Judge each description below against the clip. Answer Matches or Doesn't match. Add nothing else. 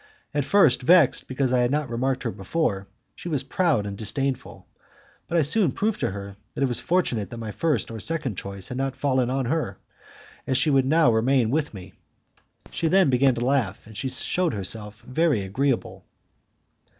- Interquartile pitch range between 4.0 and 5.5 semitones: Matches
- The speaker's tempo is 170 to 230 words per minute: Matches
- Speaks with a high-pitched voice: Doesn't match